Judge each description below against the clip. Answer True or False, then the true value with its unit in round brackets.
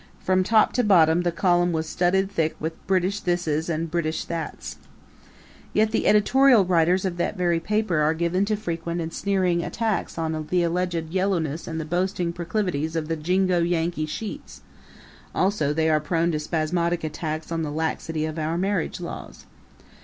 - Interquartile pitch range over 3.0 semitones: False (2.6 semitones)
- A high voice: False (170 Hz)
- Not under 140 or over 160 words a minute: False (170 wpm)